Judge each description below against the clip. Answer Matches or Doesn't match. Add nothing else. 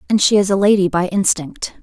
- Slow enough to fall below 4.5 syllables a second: Doesn't match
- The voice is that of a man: Doesn't match